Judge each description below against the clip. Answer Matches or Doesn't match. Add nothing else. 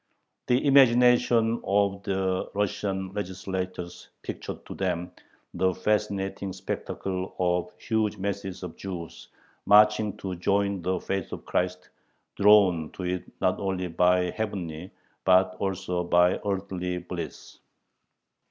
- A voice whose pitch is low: Matches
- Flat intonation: Matches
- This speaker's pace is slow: Matches